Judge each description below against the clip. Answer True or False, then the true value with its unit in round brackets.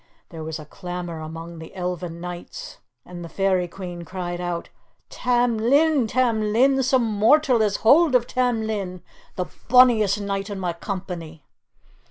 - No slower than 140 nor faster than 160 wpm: True (155 wpm)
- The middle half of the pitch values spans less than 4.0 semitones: False (5.4 semitones)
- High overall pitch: True (195 Hz)